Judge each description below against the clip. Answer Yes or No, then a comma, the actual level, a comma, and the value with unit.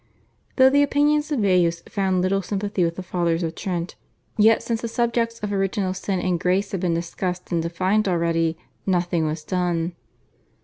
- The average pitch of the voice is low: No, medium, 185 Hz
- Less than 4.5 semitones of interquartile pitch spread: Yes, average, 3.5 semitones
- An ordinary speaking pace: Yes, average, 175 wpm